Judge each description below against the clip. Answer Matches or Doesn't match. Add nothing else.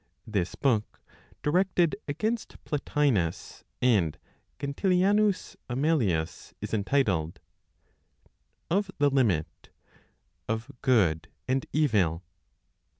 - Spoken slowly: Matches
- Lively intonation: Matches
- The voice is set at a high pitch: Doesn't match